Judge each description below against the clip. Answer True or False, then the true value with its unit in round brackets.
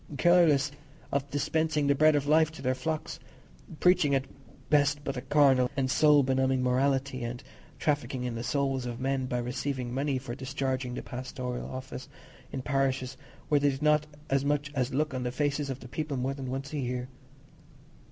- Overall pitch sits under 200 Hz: True (135 Hz)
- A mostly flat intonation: True (2.1 semitones)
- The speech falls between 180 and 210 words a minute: True (185 wpm)